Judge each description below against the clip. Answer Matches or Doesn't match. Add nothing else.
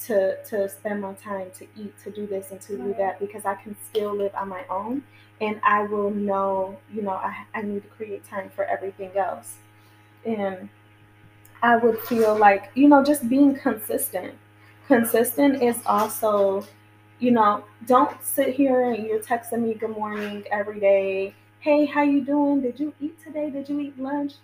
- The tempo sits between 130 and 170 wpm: Doesn't match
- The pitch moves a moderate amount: Matches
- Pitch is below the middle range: Doesn't match